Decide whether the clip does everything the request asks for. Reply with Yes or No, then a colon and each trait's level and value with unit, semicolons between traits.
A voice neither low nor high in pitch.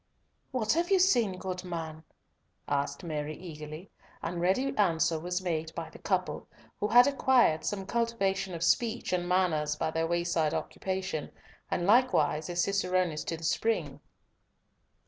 Yes: medium, 180 Hz